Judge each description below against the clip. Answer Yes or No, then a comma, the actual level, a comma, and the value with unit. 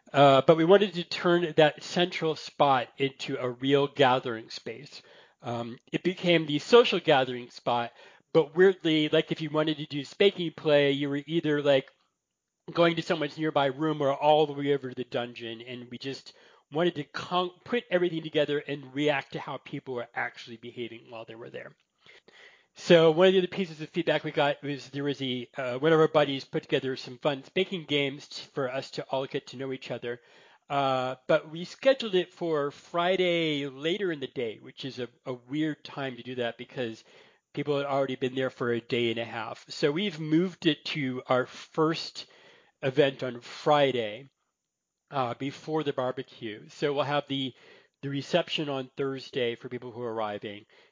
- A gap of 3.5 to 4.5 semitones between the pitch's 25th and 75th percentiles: Yes, average, 3.9 semitones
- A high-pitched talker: No, medium, 145 Hz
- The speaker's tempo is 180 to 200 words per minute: Yes, average, 190 wpm